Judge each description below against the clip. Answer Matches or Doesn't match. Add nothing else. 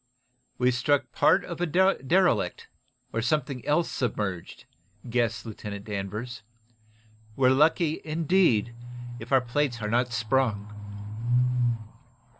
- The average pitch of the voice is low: Matches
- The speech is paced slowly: Matches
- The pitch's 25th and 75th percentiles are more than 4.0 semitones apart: Matches